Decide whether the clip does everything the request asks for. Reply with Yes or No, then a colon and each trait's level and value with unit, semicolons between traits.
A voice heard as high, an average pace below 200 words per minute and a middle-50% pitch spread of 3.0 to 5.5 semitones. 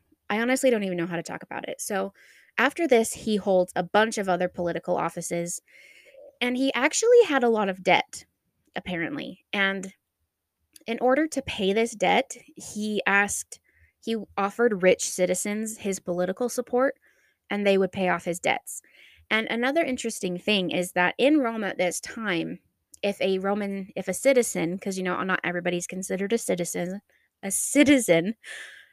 Yes: high, 195 Hz; average, 165 wpm; average, 4.5 semitones